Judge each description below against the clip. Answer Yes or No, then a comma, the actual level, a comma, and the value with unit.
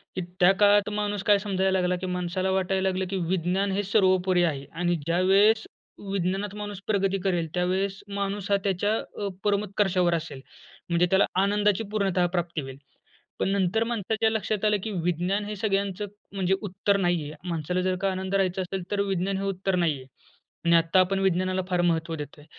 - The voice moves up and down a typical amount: No, narrow, 2.1 semitones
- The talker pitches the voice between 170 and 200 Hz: Yes, high, 190 Hz